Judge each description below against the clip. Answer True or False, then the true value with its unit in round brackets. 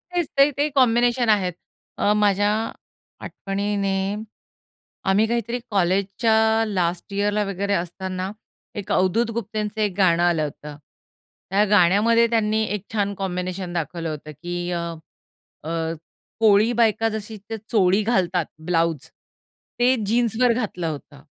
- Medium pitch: False (200 Hz)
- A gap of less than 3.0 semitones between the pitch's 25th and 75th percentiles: False (3.8 semitones)